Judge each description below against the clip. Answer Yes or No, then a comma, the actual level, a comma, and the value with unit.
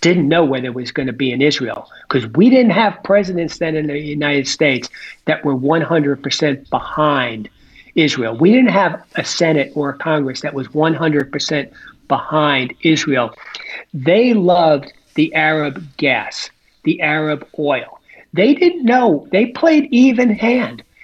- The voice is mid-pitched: Yes, medium, 155 Hz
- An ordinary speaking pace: Yes, average, 150 wpm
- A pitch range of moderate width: Yes, average, 4.3 semitones